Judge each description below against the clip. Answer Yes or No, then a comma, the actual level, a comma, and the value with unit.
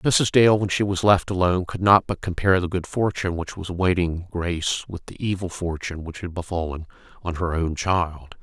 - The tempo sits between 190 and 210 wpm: Yes, fast, 205 wpm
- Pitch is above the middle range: No, very low, 90 Hz